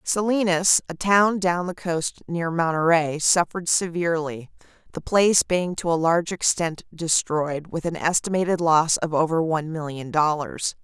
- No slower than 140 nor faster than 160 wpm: Yes, average, 150 wpm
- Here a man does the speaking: No, female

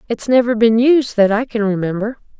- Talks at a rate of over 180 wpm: Yes, average, 200 wpm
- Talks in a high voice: Yes, high, 230 Hz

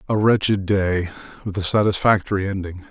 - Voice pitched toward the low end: Yes, very low, 95 Hz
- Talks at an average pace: No, slow, 125 wpm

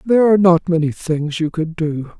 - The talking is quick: Yes, fast, 220 wpm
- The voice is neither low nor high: Yes, medium, 170 Hz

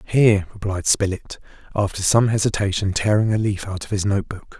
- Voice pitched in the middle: No, low, 100 Hz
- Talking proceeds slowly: No, average, 185 wpm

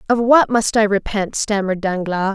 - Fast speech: No, average, 180 wpm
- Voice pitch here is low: No, high, 210 Hz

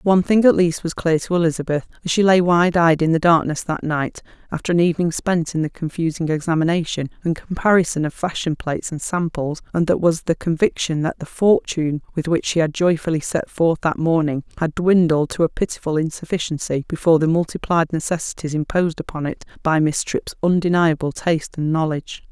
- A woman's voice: Yes, female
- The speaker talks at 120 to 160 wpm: No, average, 190 wpm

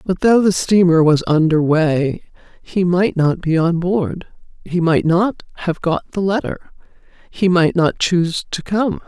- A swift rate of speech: No, average, 170 wpm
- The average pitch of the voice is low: No, medium, 175 Hz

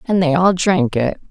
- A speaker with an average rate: No, fast, 230 wpm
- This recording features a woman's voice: Yes, female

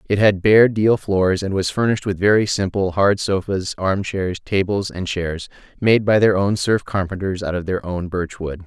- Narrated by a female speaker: No, male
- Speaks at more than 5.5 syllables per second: No, 4.6 syllables/s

